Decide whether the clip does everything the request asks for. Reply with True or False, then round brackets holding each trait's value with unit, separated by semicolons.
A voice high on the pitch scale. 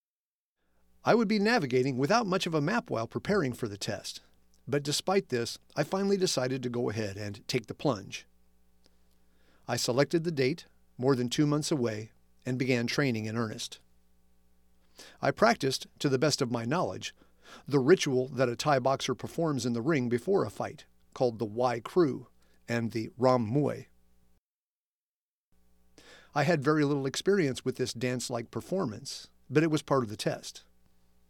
False (120 Hz)